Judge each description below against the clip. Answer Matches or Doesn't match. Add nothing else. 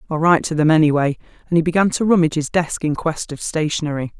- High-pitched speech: Doesn't match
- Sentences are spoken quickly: Matches